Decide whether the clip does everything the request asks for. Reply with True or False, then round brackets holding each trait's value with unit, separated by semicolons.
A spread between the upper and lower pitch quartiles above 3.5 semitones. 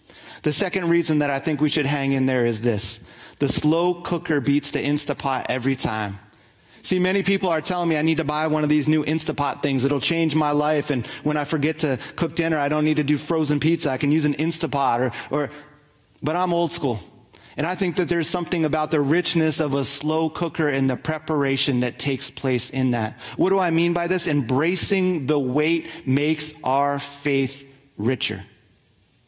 False (3.1 semitones)